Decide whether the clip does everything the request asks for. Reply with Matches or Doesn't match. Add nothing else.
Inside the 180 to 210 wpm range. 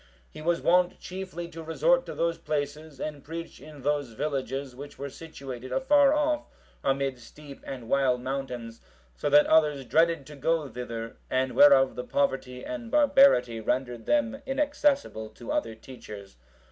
Doesn't match